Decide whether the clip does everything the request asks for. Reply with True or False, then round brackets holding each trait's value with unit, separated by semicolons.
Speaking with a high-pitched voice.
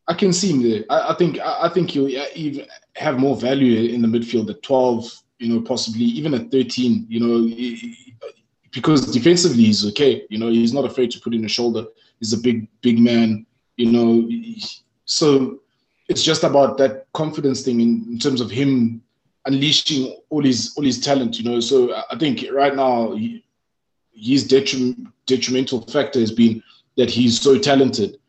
False (130 Hz)